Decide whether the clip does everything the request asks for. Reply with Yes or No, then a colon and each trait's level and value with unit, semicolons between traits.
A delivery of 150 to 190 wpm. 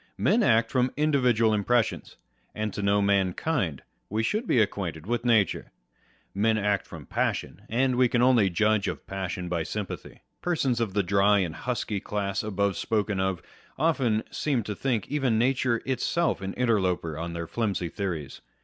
Yes: average, 165 wpm